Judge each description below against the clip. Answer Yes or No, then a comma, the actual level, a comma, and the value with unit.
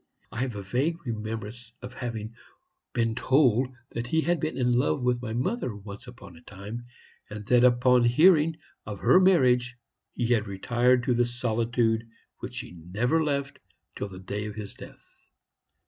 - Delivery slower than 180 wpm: Yes, average, 170 wpm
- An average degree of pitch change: Yes, average, 3.0 semitones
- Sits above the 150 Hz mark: No, low, 120 Hz